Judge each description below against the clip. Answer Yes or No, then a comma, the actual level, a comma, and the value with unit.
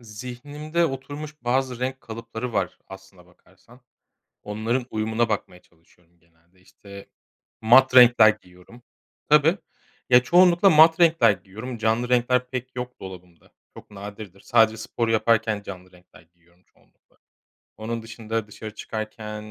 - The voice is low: Yes, low, 115 Hz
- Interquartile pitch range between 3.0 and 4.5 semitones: Yes, average, 4.2 semitones